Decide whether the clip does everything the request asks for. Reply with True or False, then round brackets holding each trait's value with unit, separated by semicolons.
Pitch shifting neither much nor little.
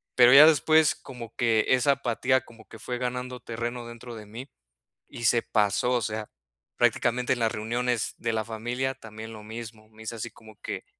False (2.0 semitones)